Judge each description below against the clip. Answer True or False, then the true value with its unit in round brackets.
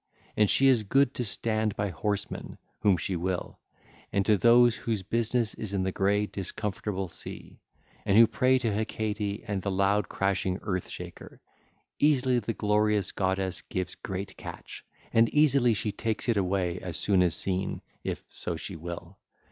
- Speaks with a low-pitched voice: True (100 Hz)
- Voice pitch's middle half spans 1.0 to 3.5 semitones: True (3.1 semitones)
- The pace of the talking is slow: False (165 wpm)